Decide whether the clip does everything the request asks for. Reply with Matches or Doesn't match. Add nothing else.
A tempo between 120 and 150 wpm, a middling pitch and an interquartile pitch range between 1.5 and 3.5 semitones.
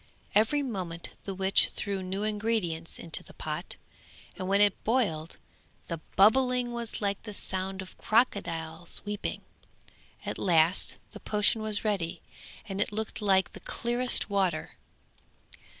Doesn't match